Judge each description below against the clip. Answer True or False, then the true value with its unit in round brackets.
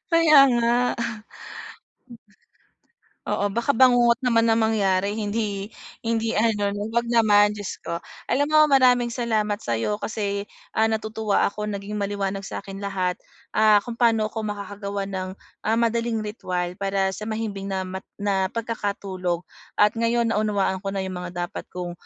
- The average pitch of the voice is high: True (210 Hz)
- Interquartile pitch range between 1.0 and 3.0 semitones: True (2.7 semitones)